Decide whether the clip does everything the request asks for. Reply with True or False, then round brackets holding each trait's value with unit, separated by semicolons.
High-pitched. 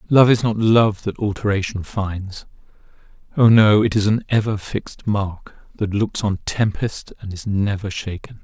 False (105 Hz)